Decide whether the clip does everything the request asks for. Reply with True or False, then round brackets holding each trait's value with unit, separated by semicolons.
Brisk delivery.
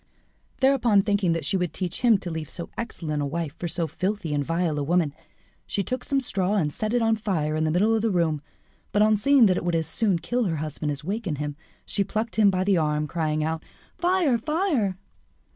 True (225 wpm)